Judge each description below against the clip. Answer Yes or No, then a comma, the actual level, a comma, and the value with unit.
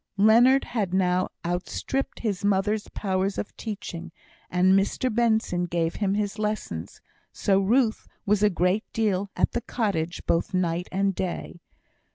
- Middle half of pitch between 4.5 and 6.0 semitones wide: No, average, 3.2 semitones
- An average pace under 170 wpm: Yes, average, 145 wpm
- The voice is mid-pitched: No, high, 195 Hz